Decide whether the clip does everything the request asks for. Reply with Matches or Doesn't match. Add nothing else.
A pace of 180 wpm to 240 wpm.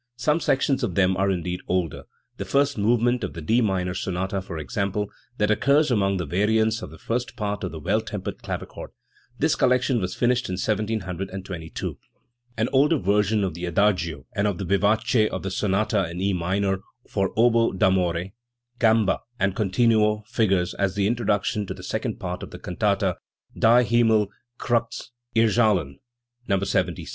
Doesn't match